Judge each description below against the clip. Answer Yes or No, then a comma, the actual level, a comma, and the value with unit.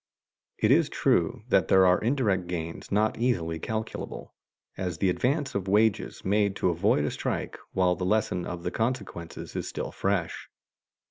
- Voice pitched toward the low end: Yes, very low, 95 Hz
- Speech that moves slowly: No, average, 160 wpm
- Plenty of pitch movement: No, average, 3.8 semitones